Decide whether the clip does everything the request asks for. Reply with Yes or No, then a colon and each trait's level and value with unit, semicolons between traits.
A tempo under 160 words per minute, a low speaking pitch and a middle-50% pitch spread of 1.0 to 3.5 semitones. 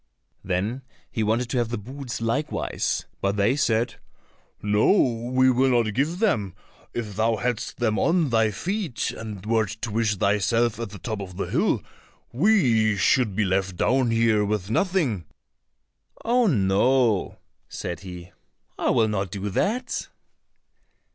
No: average, 150 wpm; low, 115 Hz; average, 3.9 semitones